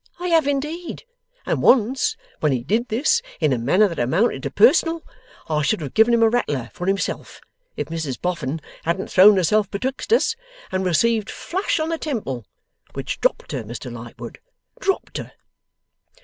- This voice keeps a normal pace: Yes, average, 170 wpm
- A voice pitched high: Yes, high, 200 Hz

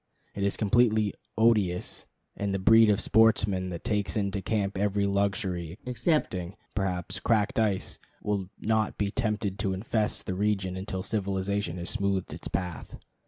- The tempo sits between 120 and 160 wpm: Yes, average, 150 wpm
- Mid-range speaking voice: No, low, 100 Hz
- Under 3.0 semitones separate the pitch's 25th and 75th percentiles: Yes, narrow, 2.4 semitones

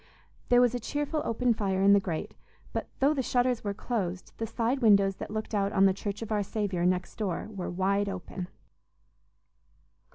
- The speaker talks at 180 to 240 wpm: Yes, average, 190 wpm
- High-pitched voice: Yes, high, 205 Hz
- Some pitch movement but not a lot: Yes, average, 3.4 semitones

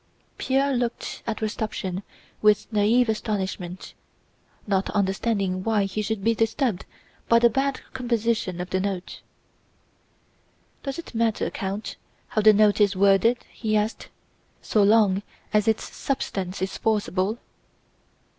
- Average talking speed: No, slow, 125 wpm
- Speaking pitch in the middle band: No, high, 215 Hz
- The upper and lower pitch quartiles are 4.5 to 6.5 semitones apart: No, average, 2.8 semitones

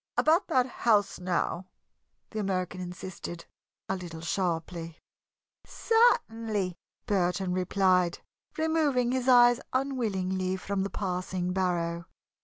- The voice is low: No, high, 190 Hz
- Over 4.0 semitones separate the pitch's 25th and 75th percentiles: Yes, average, 5.0 semitones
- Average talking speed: No, slow, 100 wpm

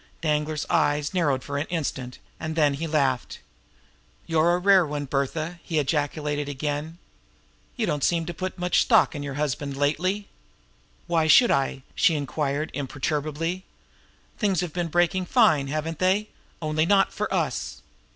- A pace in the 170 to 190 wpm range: No, average, 150 wpm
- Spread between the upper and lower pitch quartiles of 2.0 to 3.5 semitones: Yes, average, 3.2 semitones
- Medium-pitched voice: Yes, medium, 155 Hz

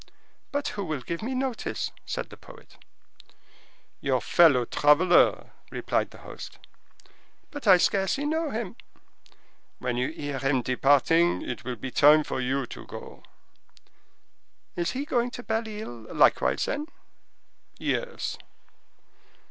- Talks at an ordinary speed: No, slow, 130 wpm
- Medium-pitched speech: Yes, medium, 170 Hz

